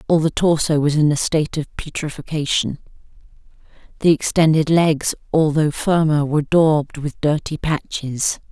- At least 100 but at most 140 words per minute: Yes, slow, 135 wpm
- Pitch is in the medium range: Yes, medium, 155 Hz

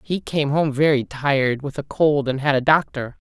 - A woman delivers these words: Yes, female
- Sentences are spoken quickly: Yes, fast, 220 wpm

